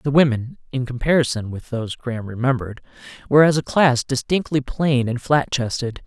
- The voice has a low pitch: Yes, low, 130 Hz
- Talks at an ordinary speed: Yes, average, 170 wpm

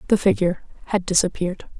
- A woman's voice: Yes, female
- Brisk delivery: No, slow, 135 wpm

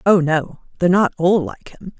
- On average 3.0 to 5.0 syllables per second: Yes, 4.9 syllables/s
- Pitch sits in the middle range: Yes, medium, 175 Hz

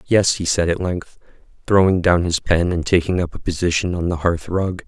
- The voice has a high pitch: No, very low, 90 Hz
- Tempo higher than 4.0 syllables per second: Yes, 5.2 syllables/s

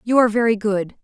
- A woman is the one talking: Yes, female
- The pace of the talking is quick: Yes, fast, 230 wpm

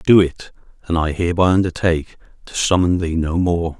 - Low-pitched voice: Yes, very low, 85 Hz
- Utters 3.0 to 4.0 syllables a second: No, 5.6 syllables/s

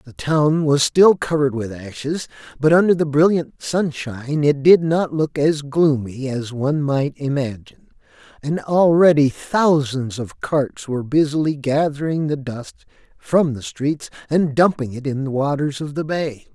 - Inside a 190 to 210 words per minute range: No, average, 160 wpm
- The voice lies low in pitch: No, medium, 145 Hz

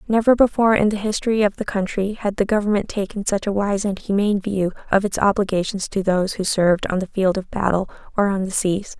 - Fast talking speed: Yes, fast, 225 wpm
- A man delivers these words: No, female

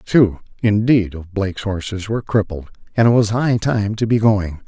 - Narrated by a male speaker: Yes, male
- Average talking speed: Yes, average, 195 wpm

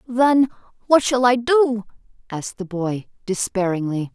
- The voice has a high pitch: Yes, high, 225 Hz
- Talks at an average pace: No, slow, 130 wpm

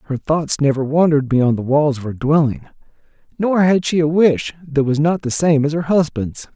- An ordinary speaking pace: No, fast, 210 wpm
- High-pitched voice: No, medium, 150 Hz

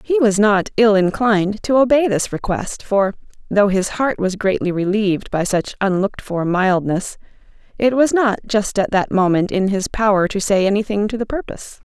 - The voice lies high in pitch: Yes, high, 205 Hz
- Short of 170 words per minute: No, average, 185 wpm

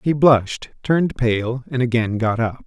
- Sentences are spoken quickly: No, average, 180 wpm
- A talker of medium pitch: No, low, 125 Hz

